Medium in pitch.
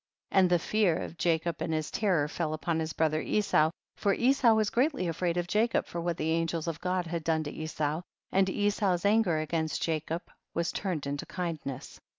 Yes: medium, 170 Hz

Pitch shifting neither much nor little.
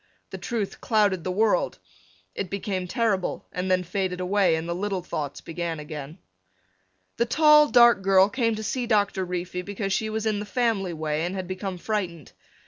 Yes: average, 3.3 semitones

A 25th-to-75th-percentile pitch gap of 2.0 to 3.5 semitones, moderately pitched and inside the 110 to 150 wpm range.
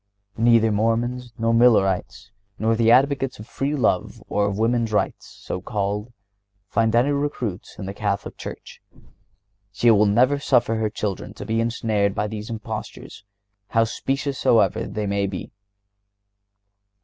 No: average, 2.7 semitones; low, 110 Hz; average, 145 wpm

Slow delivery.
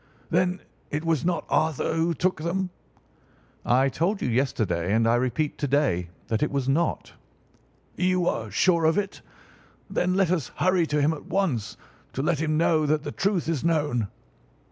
No: average, 175 wpm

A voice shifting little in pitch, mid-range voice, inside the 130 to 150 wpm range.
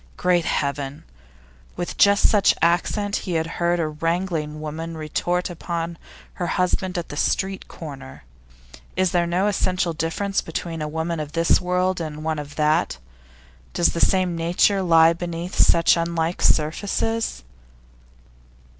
Yes: narrow, 2.2 semitones; medium, 170 Hz; average, 145 wpm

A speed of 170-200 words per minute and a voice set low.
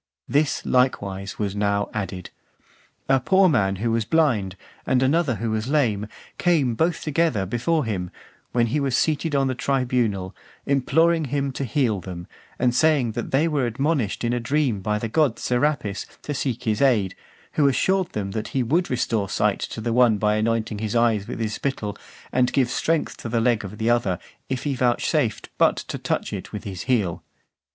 Yes: average, 190 wpm; low, 120 Hz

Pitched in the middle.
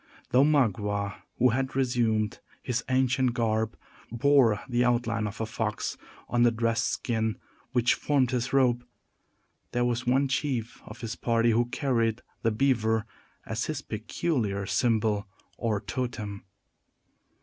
No: low, 120 Hz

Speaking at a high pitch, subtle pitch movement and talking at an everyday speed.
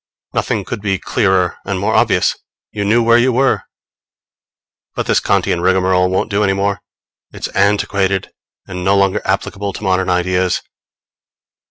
No: very low, 95 Hz; narrow, 1.6 semitones; average, 150 wpm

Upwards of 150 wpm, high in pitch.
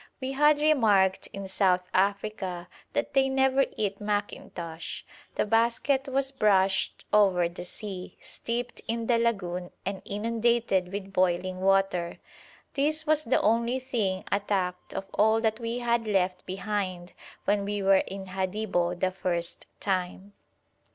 No: average, 140 wpm; high, 200 Hz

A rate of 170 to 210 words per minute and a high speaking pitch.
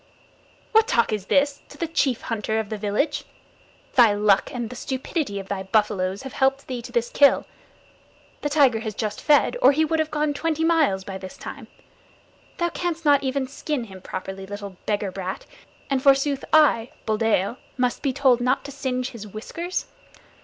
Yes: average, 180 wpm; very high, 250 Hz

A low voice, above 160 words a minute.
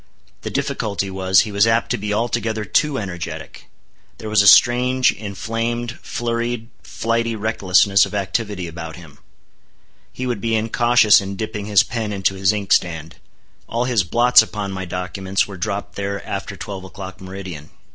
No: low, 100 Hz; average, 155 wpm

